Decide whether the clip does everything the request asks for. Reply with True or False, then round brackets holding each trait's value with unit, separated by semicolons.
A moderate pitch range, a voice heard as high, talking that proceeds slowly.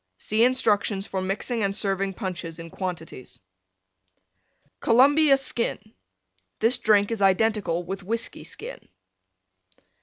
True (3.4 semitones; 200 Hz; 110 wpm)